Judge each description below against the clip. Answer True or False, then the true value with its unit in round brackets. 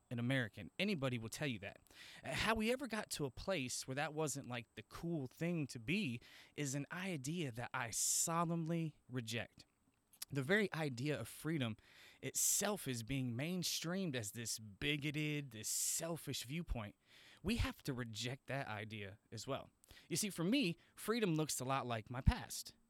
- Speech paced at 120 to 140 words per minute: False (170 wpm)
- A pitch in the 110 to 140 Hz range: True (135 Hz)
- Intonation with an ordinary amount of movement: False (5.7 semitones)